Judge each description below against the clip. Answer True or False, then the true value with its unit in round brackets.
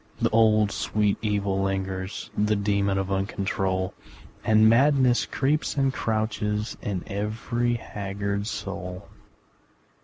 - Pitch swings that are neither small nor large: False (2.2 semitones)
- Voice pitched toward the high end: False (105 Hz)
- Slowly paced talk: True (110 wpm)